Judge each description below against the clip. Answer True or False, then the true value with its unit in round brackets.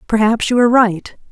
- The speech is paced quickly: False (185 wpm)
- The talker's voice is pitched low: False (225 Hz)